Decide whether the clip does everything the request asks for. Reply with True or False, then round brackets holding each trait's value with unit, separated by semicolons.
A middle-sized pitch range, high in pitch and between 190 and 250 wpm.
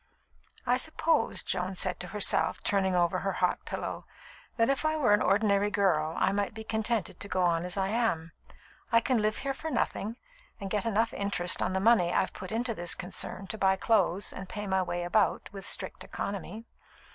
True (3.4 semitones; 200 Hz; 200 wpm)